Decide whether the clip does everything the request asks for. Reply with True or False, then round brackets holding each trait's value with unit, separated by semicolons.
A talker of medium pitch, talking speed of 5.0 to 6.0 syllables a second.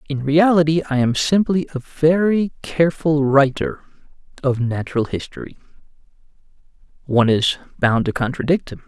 True (145 Hz; 5.2 syllables/s)